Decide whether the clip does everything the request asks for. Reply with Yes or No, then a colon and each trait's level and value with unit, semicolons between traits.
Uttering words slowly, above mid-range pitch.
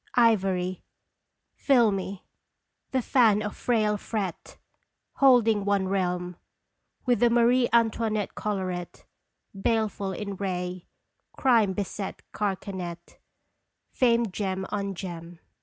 Yes: slow, 95 wpm; high, 200 Hz